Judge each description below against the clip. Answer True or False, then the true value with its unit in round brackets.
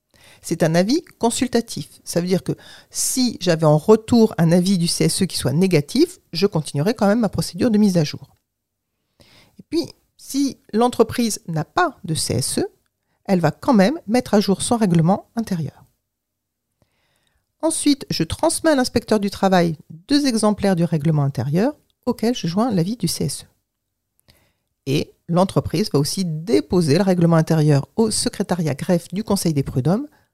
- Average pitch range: False (6.9 semitones)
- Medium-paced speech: True (160 wpm)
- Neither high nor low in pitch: True (180 Hz)